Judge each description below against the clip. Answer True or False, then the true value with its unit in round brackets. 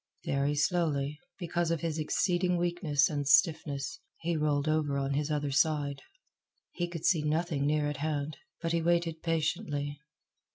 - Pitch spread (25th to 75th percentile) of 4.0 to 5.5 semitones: False (2.6 semitones)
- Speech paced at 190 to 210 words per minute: False (155 wpm)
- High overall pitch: False (155 Hz)